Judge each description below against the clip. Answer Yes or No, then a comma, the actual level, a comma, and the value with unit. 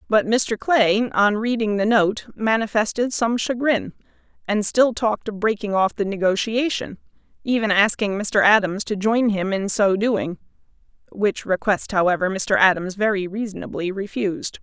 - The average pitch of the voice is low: No, high, 210 Hz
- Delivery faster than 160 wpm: No, average, 150 wpm